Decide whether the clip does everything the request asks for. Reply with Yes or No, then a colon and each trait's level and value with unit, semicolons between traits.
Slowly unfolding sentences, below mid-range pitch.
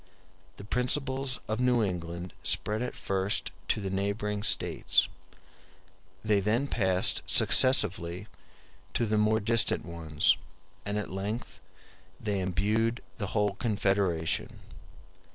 Yes: slow, 115 wpm; low, 105 Hz